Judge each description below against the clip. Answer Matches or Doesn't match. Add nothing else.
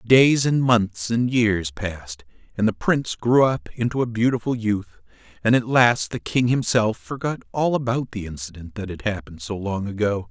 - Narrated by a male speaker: Matches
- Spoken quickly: Doesn't match